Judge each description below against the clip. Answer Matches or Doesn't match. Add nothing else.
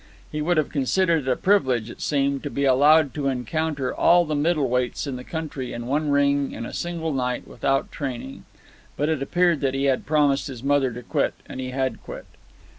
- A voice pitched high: Doesn't match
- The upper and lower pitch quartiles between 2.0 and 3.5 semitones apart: Matches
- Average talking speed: Doesn't match